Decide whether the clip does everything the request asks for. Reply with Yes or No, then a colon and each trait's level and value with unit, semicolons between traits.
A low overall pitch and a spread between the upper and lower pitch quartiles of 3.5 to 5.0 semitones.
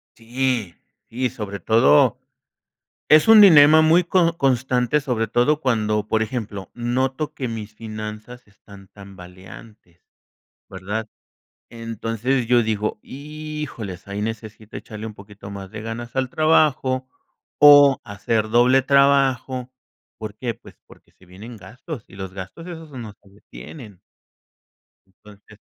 Yes: low, 115 Hz; average, 4.1 semitones